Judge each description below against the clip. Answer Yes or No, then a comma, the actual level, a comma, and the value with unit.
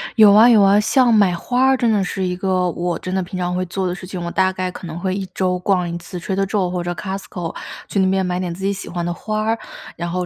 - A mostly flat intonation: Yes, narrow, 2.1 semitones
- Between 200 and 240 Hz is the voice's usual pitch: No, medium, 185 Hz